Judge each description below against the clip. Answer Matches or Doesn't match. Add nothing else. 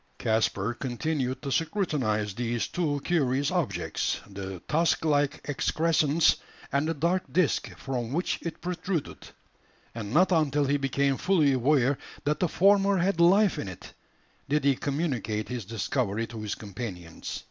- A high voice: Doesn't match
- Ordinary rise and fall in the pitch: Doesn't match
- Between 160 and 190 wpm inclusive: Doesn't match